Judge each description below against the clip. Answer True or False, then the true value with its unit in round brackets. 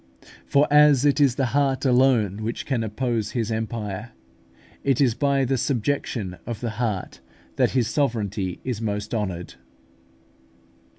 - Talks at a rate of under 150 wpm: True (140 wpm)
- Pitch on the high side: False (120 Hz)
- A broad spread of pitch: False (4.1 semitones)